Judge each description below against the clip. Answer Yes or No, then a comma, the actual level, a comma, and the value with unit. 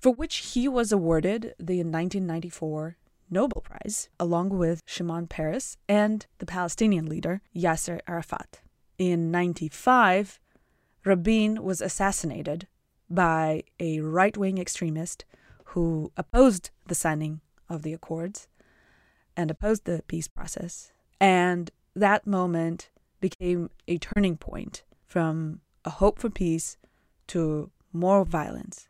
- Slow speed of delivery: Yes, slow, 115 wpm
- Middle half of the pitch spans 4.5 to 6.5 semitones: No, average, 3.1 semitones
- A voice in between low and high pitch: Yes, medium, 175 Hz